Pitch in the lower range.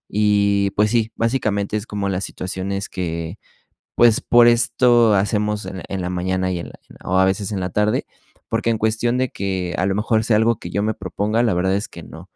Yes: low, 100 Hz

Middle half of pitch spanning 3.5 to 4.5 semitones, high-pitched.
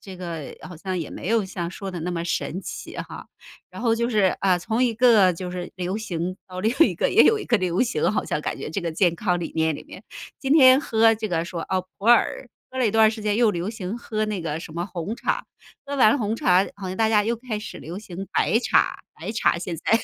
Yes: average, 4.1 semitones; high, 195 Hz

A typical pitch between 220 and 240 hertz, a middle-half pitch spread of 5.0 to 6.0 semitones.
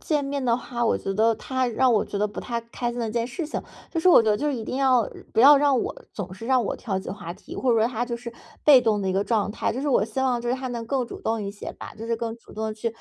No: high, 235 Hz; average, 2.9 semitones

